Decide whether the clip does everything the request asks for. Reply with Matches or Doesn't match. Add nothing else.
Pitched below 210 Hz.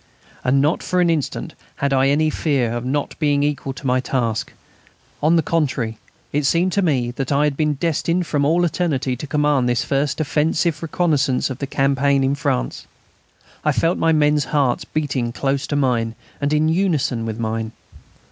Matches